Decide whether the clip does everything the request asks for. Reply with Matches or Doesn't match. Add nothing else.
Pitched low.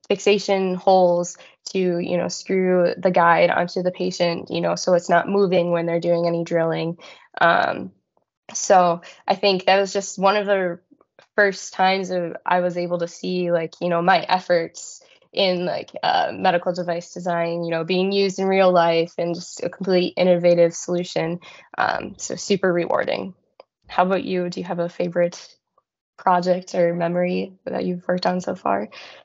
Doesn't match